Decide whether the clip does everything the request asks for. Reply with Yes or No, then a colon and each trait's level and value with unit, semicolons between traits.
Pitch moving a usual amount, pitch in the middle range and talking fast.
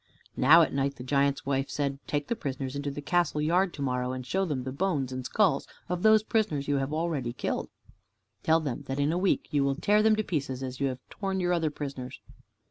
Yes: average, 4.5 semitones; medium, 145 Hz; fast, 230 wpm